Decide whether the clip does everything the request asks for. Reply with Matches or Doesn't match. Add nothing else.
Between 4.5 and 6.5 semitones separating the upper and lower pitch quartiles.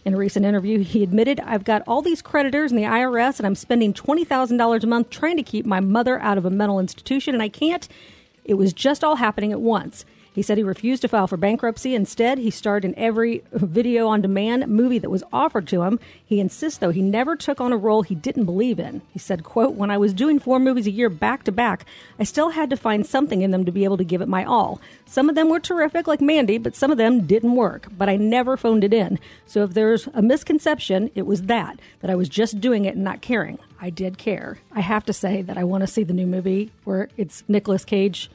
Doesn't match